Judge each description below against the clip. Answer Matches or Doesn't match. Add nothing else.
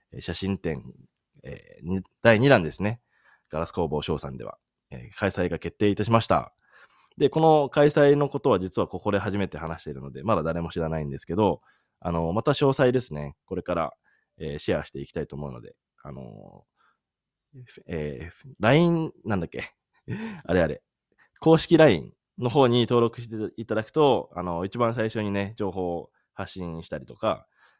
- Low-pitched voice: Matches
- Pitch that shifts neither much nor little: Doesn't match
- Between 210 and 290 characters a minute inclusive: Doesn't match